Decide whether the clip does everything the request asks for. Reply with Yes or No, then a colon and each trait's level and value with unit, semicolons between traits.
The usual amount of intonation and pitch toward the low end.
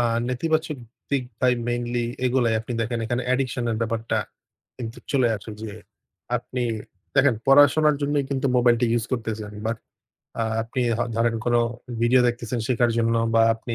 No: narrow, 2.0 semitones; low, 120 Hz